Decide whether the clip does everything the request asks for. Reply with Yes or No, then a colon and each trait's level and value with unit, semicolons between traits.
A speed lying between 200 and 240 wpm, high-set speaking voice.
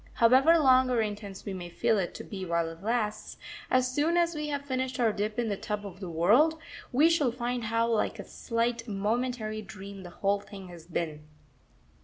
Yes: fast, 205 wpm; high, 220 Hz